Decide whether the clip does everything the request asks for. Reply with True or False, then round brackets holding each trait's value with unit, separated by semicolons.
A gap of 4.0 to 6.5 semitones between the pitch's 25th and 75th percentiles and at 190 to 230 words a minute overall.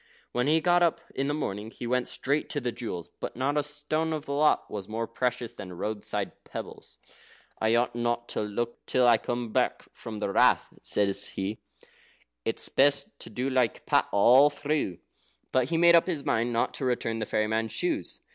True (4.6 semitones; 195 wpm)